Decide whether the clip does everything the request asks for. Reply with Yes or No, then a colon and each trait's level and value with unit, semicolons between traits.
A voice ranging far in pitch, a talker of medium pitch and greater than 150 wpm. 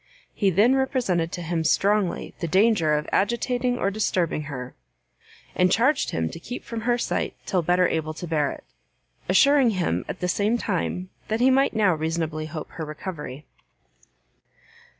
Yes: wide, 6.2 semitones; medium, 180 Hz; average, 165 wpm